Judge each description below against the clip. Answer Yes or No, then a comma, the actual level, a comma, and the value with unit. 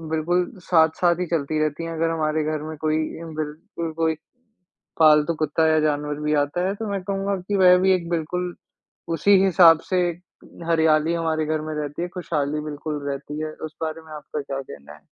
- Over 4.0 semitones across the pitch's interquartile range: No, narrow, 2.4 semitones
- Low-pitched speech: No, medium, 160 Hz